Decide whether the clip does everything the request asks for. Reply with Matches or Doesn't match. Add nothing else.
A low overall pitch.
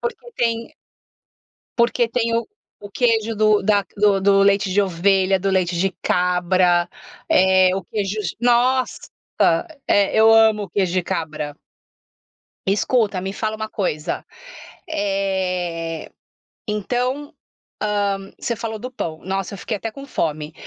Doesn't match